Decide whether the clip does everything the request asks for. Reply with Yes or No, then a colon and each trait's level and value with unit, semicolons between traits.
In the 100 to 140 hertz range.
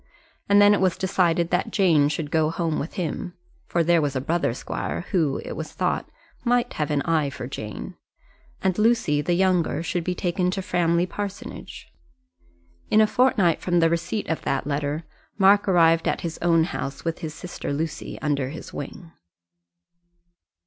No: medium, 170 Hz